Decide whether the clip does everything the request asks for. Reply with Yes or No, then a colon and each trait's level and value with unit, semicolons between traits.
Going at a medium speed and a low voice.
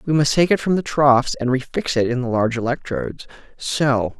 No: fast, 215 wpm; low, 130 Hz